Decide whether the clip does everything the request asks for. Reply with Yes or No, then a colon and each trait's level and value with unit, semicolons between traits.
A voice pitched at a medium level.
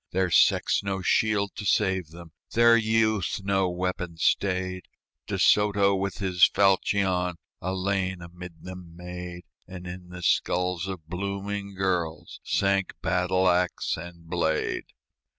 No: very low, 95 Hz